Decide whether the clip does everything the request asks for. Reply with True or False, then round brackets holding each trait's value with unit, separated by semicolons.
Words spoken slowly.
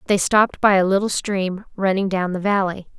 False (200 wpm)